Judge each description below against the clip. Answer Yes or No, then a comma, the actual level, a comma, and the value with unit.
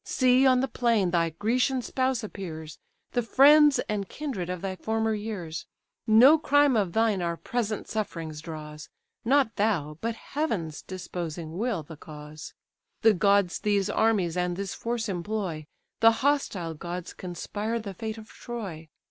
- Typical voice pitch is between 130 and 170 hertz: No, high, 205 Hz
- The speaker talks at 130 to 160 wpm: Yes, average, 150 wpm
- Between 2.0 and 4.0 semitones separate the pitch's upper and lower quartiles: No, average, 5.3 semitones